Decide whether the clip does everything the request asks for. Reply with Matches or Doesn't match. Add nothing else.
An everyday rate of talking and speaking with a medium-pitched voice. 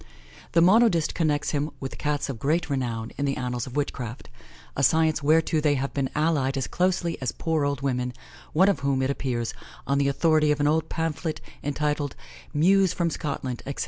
Matches